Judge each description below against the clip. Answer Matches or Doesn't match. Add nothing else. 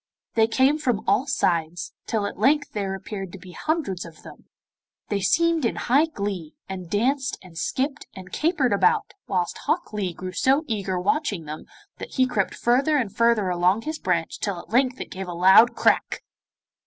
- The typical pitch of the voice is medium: Doesn't match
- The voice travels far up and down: Matches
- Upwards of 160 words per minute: Matches